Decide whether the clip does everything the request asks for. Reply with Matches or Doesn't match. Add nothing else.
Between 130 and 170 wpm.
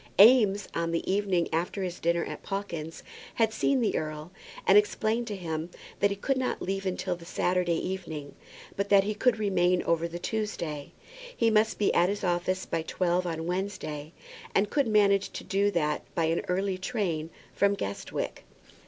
Doesn't match